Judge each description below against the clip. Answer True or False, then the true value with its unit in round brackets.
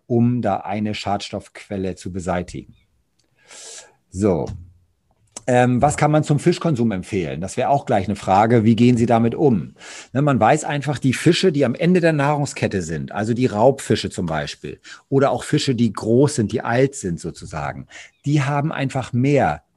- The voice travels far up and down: True (5.8 semitones)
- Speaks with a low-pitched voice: True (120 Hz)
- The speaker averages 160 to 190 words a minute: True (170 wpm)